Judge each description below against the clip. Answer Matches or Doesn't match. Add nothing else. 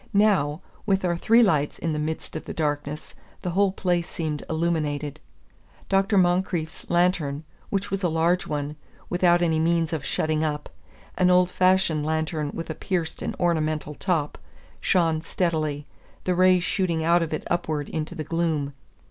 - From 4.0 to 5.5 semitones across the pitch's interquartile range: Doesn't match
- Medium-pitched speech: Matches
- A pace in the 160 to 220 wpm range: Matches